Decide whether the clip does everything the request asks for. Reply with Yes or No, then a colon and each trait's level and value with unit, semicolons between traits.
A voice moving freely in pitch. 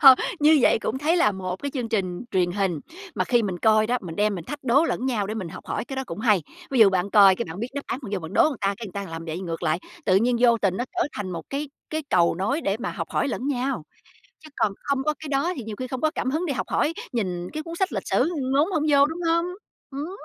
Yes: wide, 6.9 semitones